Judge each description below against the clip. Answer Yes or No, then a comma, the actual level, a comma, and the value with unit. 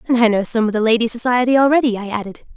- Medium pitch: No, high, 230 Hz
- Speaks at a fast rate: Yes, fast, 260 wpm